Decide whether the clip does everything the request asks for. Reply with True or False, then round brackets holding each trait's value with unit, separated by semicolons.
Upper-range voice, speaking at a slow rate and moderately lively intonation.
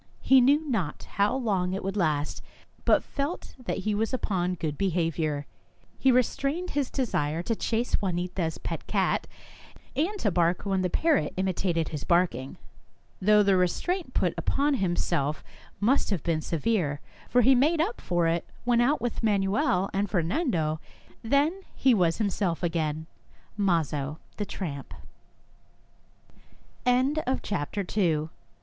False (195 Hz; 120 wpm; 6.6 semitones)